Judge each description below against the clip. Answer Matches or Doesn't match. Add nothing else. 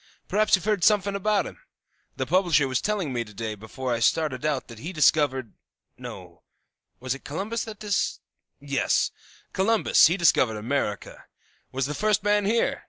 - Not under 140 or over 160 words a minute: Doesn't match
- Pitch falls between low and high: Matches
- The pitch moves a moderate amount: Doesn't match